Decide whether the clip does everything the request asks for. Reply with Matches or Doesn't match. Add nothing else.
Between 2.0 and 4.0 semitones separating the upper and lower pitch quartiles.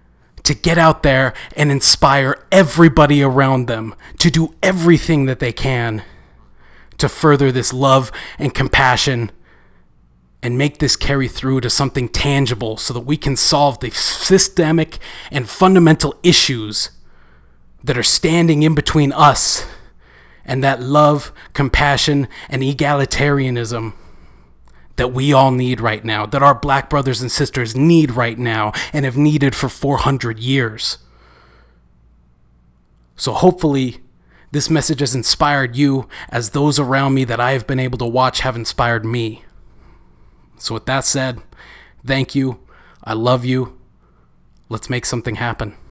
Doesn't match